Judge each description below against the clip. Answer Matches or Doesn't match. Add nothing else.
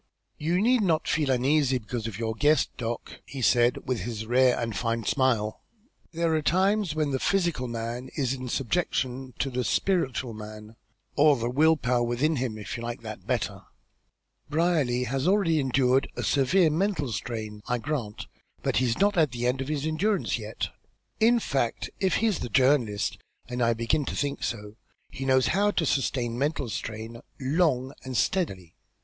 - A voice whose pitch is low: Matches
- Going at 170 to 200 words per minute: Matches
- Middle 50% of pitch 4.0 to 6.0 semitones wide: Matches